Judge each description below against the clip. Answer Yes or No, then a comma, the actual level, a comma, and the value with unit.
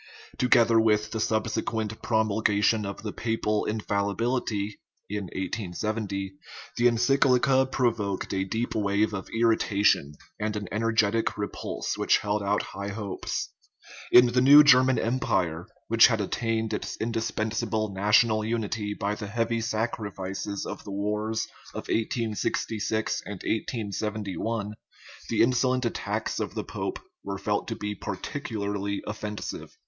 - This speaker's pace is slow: Yes, slow, 130 wpm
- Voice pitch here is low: Yes, low, 110 Hz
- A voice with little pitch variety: Yes, narrow, 2.1 semitones